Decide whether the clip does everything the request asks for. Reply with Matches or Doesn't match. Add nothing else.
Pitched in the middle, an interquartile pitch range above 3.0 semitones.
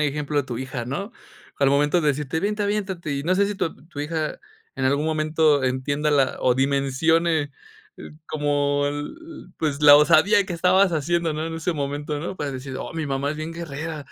Doesn't match